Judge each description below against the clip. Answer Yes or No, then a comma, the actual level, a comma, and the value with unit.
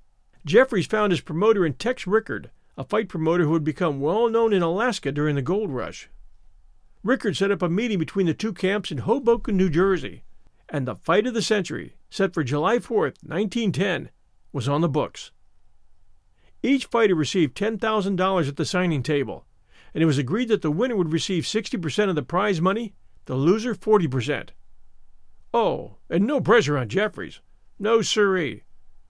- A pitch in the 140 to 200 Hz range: Yes, medium, 185 Hz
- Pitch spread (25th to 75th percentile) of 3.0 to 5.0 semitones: No, wide, 5.6 semitones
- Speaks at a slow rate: No, average, 170 wpm